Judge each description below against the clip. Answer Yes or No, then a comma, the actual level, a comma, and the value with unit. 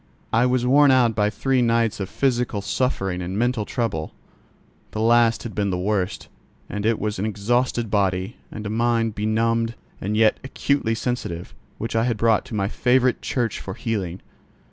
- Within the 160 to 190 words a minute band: Yes, average, 175 wpm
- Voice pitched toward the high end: No, low, 115 Hz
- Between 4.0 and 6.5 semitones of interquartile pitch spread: No, average, 2.7 semitones